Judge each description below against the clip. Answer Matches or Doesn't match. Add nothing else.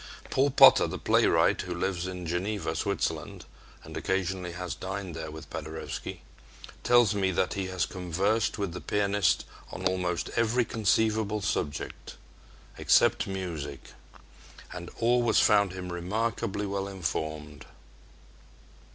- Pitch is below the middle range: Matches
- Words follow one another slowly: Matches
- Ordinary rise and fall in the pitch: Matches